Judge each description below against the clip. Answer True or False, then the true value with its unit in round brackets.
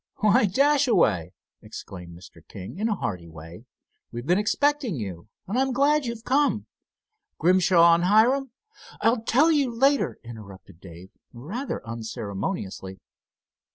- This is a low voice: False (185 Hz)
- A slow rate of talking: True (125 wpm)